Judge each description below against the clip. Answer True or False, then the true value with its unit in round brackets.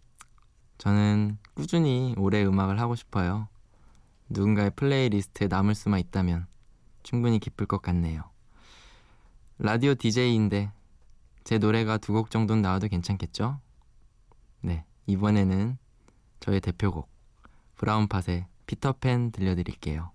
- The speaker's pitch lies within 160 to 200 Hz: False (105 Hz)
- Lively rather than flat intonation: False (2.8 semitones)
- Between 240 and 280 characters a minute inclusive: True (265 characters per minute)